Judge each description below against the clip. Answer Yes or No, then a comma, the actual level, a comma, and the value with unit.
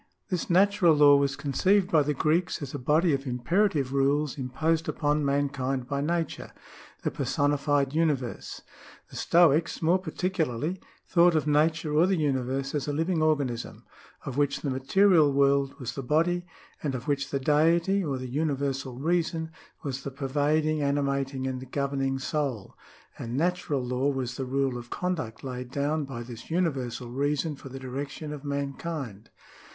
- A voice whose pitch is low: No, medium, 145 Hz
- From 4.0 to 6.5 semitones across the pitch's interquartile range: No, average, 3.0 semitones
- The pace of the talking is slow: No, average, 160 wpm